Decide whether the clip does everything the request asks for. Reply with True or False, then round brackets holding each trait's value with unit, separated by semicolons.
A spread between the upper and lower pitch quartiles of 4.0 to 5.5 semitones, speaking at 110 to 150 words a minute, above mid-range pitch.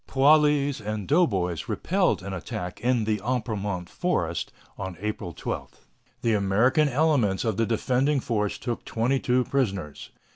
False (5.1 semitones; 140 wpm; 115 Hz)